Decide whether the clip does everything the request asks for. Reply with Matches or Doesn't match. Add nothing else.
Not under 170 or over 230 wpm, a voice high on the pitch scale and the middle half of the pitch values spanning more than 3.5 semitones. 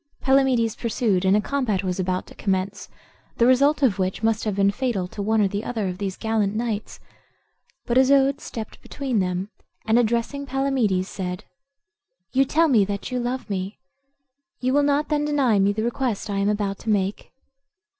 Matches